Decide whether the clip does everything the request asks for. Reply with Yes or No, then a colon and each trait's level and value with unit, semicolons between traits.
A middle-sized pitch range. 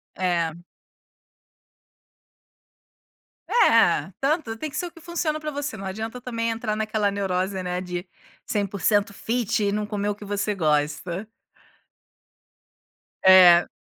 Yes: average, 3.5 semitones